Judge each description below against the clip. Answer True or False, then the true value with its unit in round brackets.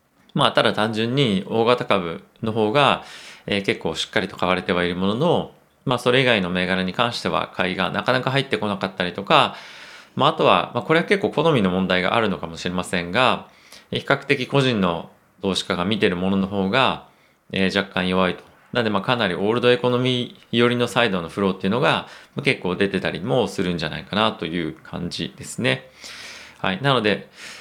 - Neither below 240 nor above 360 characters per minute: False (390 characters per minute)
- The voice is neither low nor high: False (100 Hz)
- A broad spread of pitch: False (4.8 semitones)